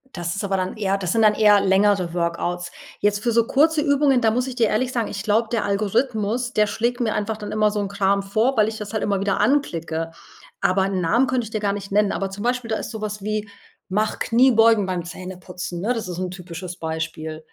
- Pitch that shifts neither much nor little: Yes, average, 3.2 semitones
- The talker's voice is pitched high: Yes, high, 205 Hz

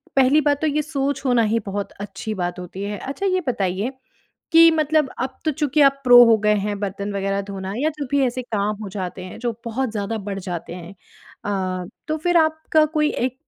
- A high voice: Yes, high, 235 Hz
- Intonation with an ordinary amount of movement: No, wide, 6.4 semitones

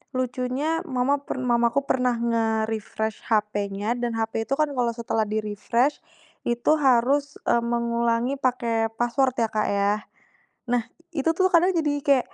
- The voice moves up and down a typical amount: Yes, average, 3.3 semitones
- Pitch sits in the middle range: No, high, 240 Hz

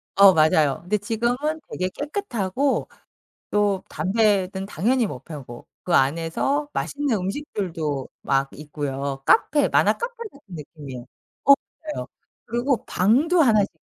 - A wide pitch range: Yes, wide, 8.4 semitones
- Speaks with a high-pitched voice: Yes, high, 195 Hz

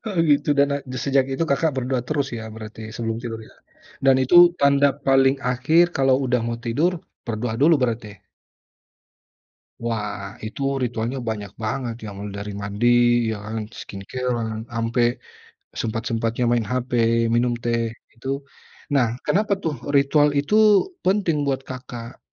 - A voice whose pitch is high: No, low, 125 Hz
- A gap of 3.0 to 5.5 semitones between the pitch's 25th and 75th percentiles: Yes, average, 3.7 semitones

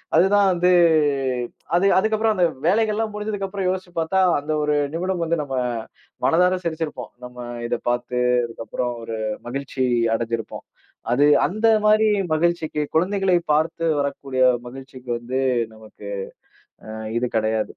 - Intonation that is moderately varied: No, wide, 7.1 semitones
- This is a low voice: No, medium, 160 Hz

